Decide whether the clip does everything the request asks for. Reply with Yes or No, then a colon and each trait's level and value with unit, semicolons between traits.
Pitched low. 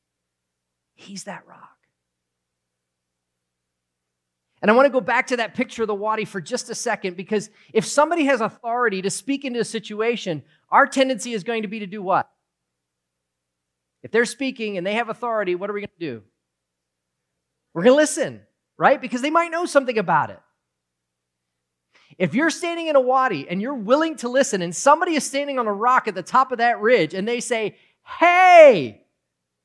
No: high, 210 Hz